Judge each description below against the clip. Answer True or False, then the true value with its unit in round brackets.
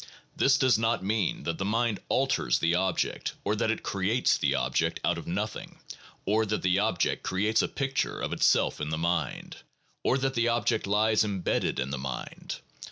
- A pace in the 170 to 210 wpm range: True (185 wpm)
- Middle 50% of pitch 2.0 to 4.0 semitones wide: False (4.5 semitones)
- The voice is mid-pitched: False (105 Hz)